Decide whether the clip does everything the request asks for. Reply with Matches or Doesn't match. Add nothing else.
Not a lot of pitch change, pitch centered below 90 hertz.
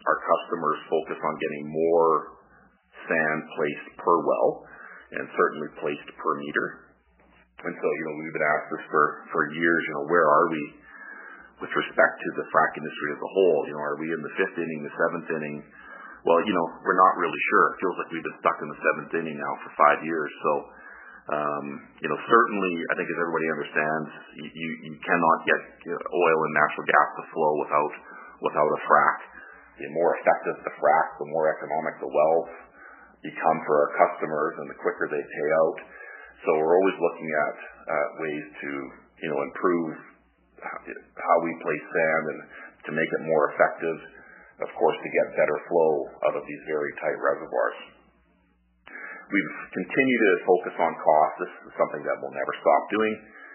Matches